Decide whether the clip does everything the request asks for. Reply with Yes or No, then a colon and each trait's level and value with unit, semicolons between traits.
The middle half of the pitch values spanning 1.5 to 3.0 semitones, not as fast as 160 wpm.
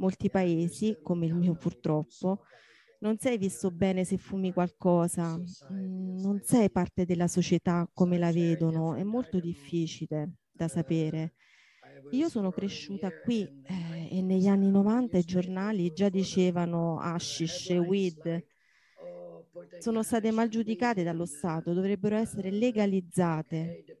Yes: average, 2.7 semitones; average, 125 wpm